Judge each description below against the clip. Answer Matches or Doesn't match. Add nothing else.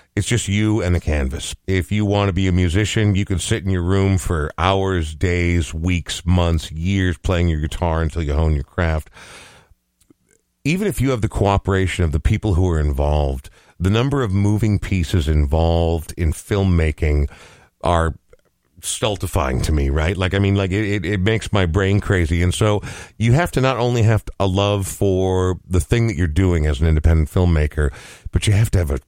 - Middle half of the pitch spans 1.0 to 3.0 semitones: Doesn't match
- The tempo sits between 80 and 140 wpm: Doesn't match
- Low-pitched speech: Matches